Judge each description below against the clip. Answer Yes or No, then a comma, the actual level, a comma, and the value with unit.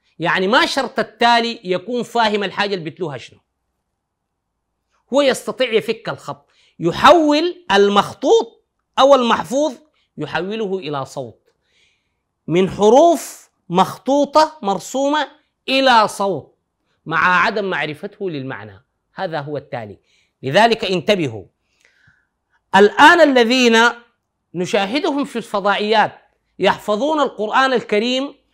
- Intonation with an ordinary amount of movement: No, wide, 8.5 semitones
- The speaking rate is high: No, average, 95 wpm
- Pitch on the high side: Yes, high, 210 Hz